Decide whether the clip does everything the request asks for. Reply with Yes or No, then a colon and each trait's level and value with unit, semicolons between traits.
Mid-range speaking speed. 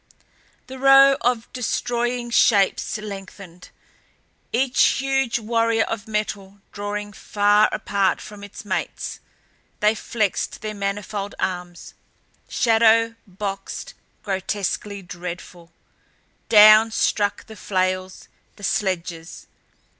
No: slow, 95 wpm